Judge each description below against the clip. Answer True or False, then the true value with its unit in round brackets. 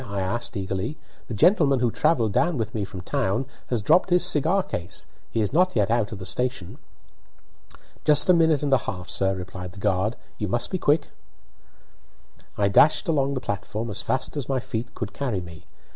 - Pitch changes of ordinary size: False (6.6 semitones)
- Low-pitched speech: True (115 Hz)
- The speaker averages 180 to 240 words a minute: True (195 wpm)